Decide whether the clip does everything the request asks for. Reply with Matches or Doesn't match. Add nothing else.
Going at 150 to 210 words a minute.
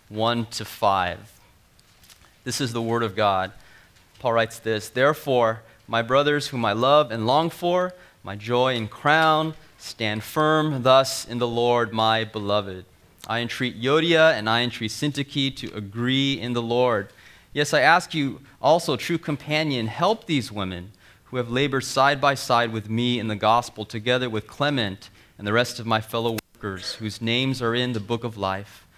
Matches